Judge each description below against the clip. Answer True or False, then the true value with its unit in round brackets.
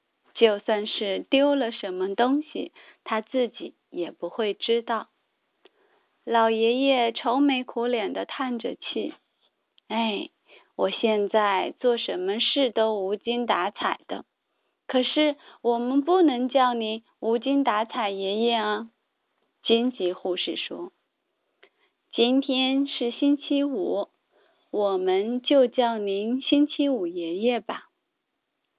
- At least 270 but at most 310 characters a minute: False (165 characters per minute)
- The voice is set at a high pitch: True (235 Hz)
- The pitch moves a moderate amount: True (3.7 semitones)